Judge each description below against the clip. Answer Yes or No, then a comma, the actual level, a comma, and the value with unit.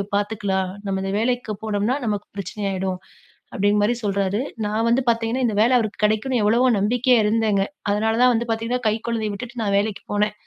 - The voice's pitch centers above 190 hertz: Yes, high, 215 Hz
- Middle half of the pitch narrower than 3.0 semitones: Yes, narrow, 2.5 semitones